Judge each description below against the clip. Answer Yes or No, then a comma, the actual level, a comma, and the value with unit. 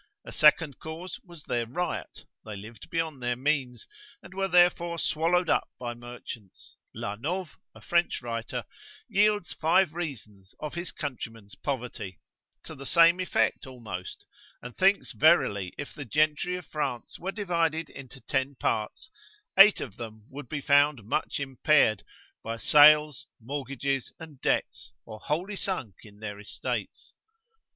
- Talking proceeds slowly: No, average, 145 wpm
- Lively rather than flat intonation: Yes, wide, 6.2 semitones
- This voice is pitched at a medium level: Yes, medium, 145 Hz